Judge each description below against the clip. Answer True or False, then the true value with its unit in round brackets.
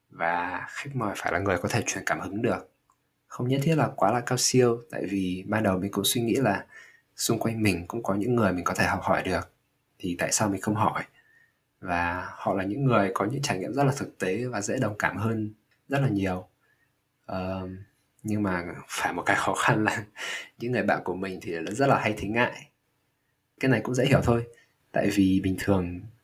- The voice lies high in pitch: False (105 Hz)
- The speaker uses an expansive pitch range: False (4.3 semitones)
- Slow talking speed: False (225 wpm)